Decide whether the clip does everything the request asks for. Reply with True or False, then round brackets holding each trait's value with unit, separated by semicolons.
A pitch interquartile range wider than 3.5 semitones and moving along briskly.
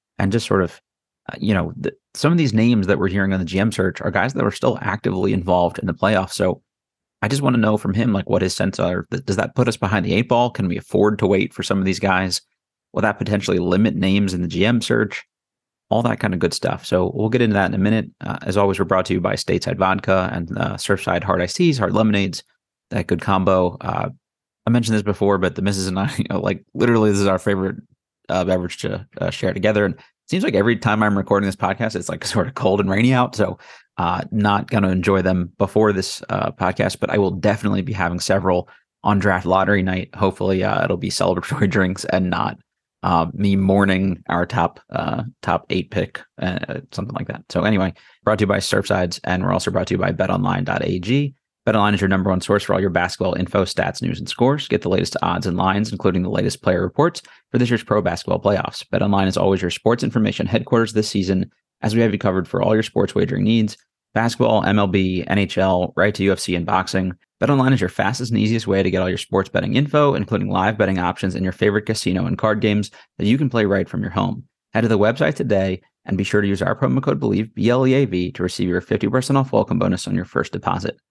False (2.7 semitones; 245 wpm)